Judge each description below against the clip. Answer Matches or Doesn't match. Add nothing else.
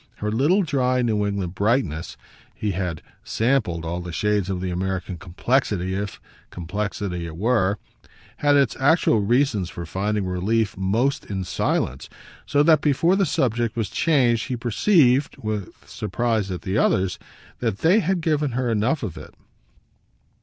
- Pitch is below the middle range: Matches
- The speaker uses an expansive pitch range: Matches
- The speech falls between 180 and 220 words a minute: Doesn't match